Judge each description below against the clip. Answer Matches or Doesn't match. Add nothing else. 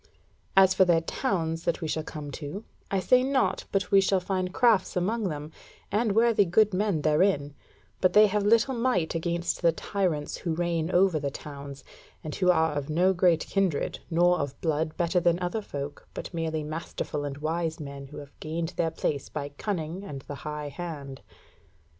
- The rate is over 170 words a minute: Matches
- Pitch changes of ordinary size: Matches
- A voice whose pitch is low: Doesn't match